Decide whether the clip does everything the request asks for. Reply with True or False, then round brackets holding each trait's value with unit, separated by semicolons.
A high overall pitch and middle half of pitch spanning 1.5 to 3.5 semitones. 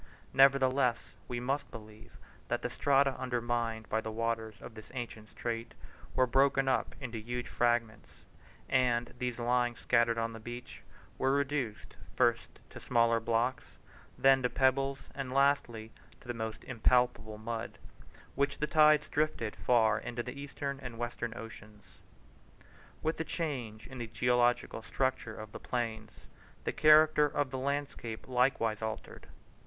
False (120 Hz; 2.9 semitones)